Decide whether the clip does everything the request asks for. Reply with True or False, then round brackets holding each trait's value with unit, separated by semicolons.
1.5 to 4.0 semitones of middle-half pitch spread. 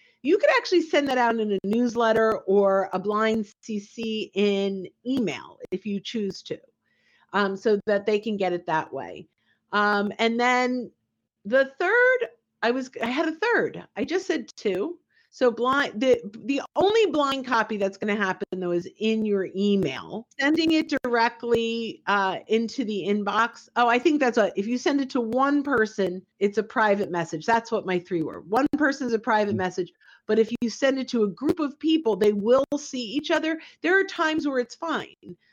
False (5.2 semitones)